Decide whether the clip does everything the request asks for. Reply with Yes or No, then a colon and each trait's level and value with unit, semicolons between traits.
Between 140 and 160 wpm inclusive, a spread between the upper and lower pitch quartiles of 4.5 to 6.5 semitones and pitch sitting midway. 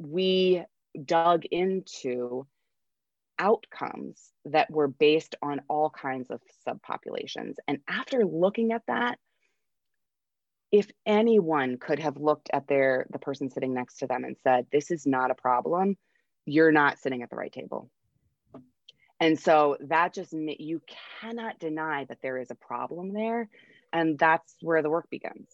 Yes: average, 150 wpm; average, 5.2 semitones; medium, 160 Hz